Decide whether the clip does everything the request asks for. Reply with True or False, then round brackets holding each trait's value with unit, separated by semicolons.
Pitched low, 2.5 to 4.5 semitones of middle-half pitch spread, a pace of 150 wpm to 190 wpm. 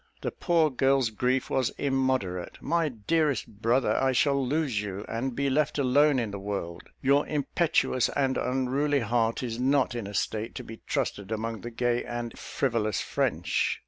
True (125 Hz; 3.6 semitones; 170 wpm)